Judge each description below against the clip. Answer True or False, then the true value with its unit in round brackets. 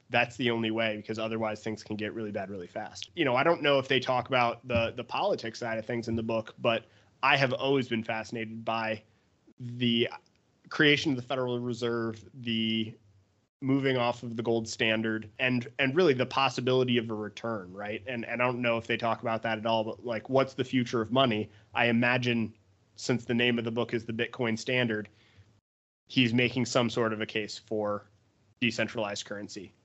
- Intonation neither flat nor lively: False (1.9 semitones)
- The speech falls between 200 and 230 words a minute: True (205 wpm)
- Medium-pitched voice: False (115 Hz)